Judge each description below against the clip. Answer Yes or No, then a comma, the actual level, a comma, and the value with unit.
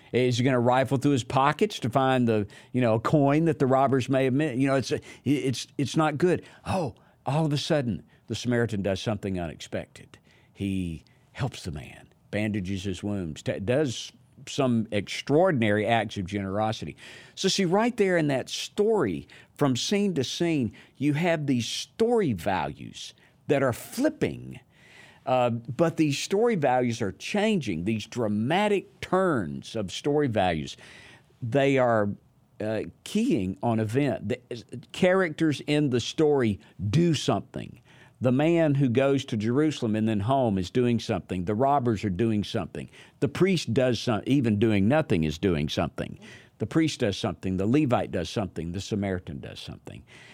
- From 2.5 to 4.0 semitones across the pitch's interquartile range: No, wide, 5.4 semitones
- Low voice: Yes, low, 125 Hz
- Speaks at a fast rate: No, average, 160 wpm